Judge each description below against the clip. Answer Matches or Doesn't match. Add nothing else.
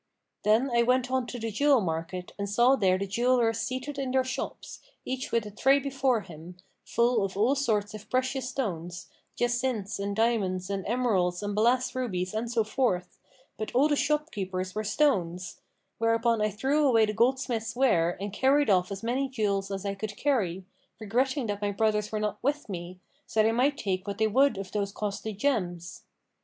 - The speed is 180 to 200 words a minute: Matches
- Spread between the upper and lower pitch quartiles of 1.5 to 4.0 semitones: Doesn't match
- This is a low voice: Doesn't match